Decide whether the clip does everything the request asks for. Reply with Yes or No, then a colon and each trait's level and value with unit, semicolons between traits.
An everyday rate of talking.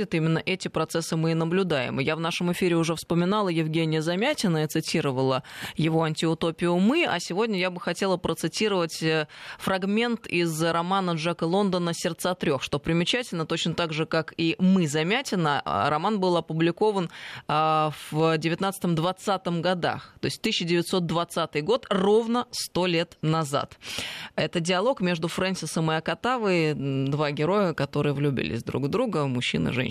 Yes: average, 140 wpm